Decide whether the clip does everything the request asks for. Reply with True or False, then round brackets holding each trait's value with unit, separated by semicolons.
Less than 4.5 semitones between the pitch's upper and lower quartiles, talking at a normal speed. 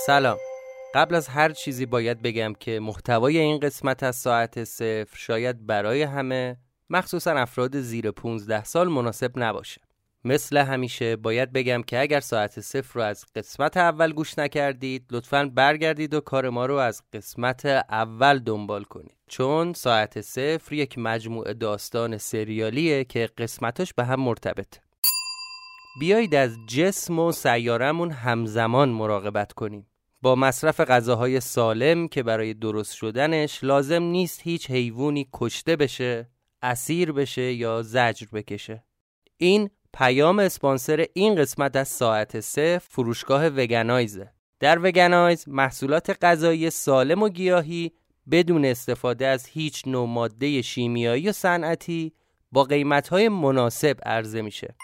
False (5.2 semitones; 130 wpm)